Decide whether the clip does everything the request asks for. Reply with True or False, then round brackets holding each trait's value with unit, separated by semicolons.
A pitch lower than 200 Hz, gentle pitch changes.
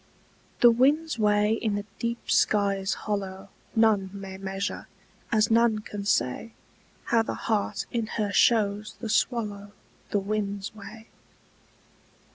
False (210 Hz; 2.1 semitones)